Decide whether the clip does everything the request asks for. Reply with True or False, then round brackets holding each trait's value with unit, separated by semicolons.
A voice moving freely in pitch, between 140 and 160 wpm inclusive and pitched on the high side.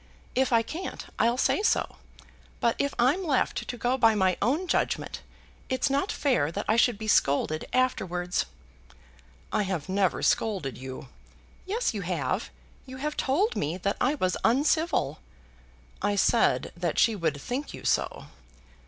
True (6.8 semitones; 155 wpm; 230 Hz)